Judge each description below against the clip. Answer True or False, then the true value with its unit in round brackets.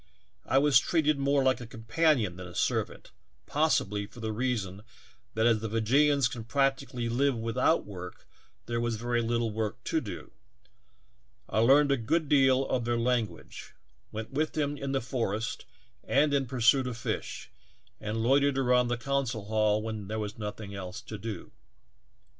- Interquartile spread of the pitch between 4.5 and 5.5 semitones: False (3.7 semitones)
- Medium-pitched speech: False (120 Hz)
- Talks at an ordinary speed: True (170 wpm)